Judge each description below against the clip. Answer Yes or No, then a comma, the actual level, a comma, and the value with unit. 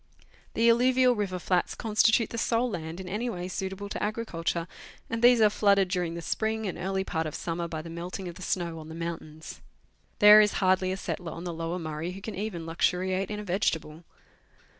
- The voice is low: No, medium, 185 Hz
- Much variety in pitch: No, average, 3.9 semitones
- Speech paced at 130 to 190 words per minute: No, fast, 205 wpm